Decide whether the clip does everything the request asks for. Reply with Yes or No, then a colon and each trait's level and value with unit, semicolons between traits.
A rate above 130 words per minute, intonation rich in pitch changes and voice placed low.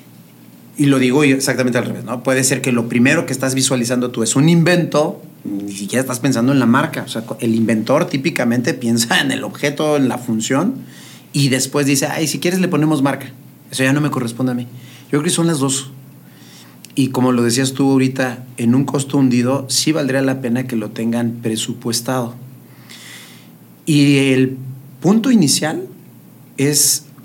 No: average, 185 wpm; narrow, 2.6 semitones; low, 130 Hz